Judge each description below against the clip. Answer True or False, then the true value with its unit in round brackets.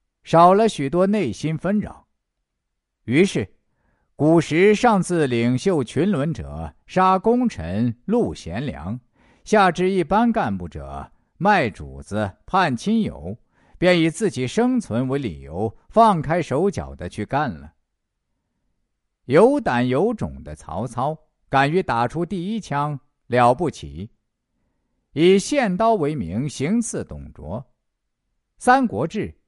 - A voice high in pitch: False (145 Hz)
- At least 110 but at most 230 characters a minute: True (170 characters per minute)